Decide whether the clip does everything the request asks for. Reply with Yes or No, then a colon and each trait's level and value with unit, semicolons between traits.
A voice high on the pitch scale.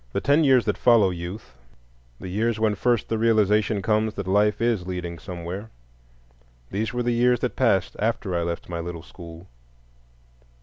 No: low, 100 Hz